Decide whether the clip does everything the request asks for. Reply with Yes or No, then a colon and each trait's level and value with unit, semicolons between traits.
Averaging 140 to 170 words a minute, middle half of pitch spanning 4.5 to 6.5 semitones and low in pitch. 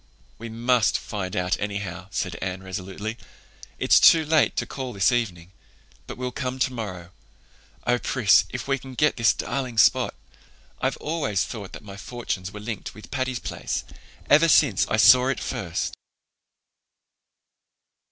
Yes: average, 150 wpm; average, 5.0 semitones; low, 115 Hz